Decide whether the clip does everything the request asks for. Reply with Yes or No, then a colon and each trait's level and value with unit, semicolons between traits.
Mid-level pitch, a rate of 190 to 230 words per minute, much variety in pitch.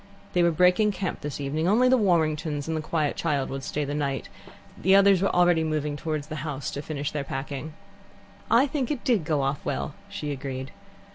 No: medium, 155 Hz; fast, 205 wpm; average, 4.1 semitones